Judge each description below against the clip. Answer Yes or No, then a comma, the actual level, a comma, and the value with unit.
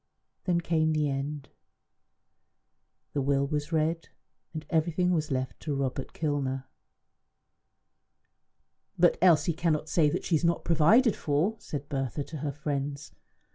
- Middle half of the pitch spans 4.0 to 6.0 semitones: No, average, 2.8 semitones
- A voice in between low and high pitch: Yes, medium, 150 Hz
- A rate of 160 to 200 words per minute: No, slow, 135 wpm